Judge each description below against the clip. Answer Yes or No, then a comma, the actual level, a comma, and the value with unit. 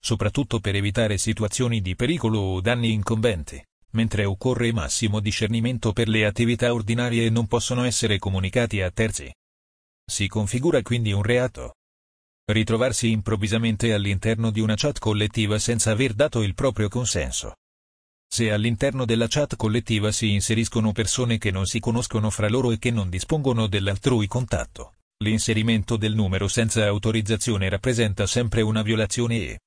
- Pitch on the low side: Yes, low, 110 Hz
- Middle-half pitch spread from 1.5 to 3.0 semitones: Yes, narrow, 2.4 semitones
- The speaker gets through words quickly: No, average, 145 wpm